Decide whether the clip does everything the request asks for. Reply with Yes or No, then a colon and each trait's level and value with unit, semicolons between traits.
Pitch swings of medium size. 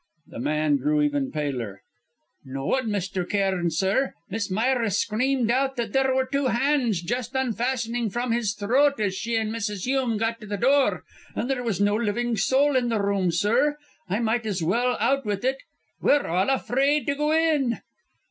Yes: average, 5.0 semitones